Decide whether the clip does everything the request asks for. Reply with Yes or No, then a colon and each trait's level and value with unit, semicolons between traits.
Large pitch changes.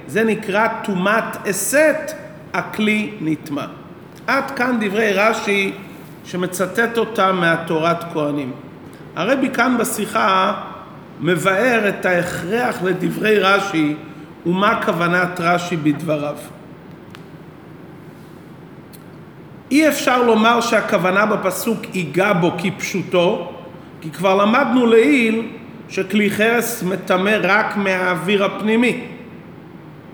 No: average, 4.2 semitones